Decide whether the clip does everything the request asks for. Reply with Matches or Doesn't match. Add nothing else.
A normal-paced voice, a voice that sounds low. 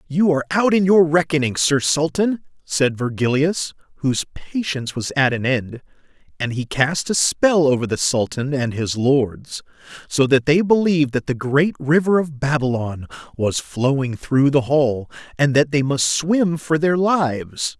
Doesn't match